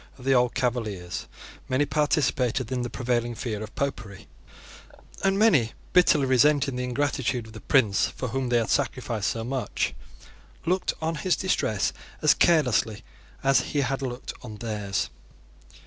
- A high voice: No, low, 125 Hz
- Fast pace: No, average, 150 wpm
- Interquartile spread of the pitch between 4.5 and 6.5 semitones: No, average, 3.6 semitones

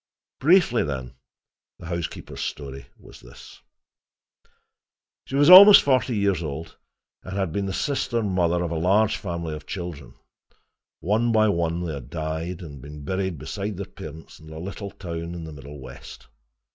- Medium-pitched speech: No, very low, 85 Hz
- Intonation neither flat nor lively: Yes, average, 4.3 semitones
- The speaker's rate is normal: Yes, average, 160 wpm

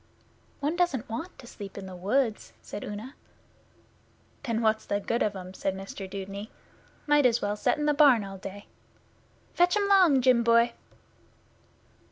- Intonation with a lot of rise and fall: Yes, wide, 5.9 semitones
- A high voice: Yes, high, 230 Hz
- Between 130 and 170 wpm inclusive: Yes, average, 165 wpm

